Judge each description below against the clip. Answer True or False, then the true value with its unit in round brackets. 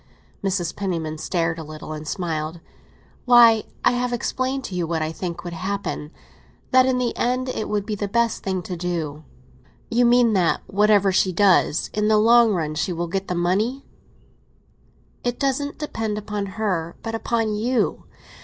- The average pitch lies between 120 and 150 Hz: False (200 Hz)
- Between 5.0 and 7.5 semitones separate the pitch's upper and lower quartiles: True (5.4 semitones)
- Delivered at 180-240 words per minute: False (170 wpm)